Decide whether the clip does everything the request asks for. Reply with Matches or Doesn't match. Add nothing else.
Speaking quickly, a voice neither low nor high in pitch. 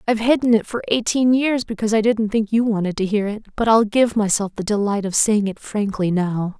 Doesn't match